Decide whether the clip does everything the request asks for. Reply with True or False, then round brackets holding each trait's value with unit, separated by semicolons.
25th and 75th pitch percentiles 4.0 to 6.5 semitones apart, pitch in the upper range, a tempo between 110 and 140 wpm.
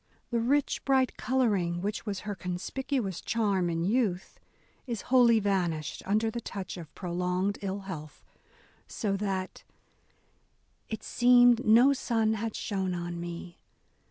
True (4.5 semitones; 200 Hz; 135 wpm)